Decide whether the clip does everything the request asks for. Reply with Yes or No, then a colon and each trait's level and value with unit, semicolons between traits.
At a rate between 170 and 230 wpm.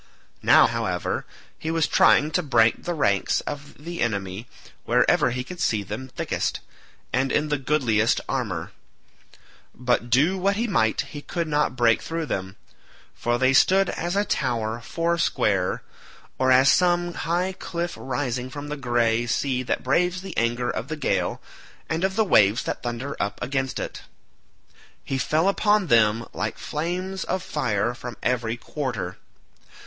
No: average, 155 wpm